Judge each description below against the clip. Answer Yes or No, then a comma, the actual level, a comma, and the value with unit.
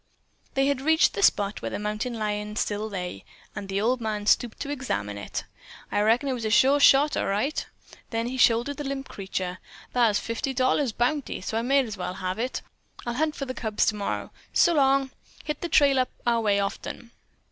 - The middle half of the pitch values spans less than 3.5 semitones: No, average, 4.5 semitones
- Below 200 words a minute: No, fast, 205 wpm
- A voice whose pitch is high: Yes, high, 235 Hz